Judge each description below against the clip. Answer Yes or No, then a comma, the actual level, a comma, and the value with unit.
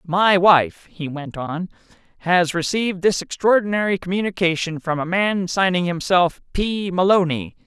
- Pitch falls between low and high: Yes, medium, 180 Hz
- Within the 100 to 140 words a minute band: Yes, slow, 135 wpm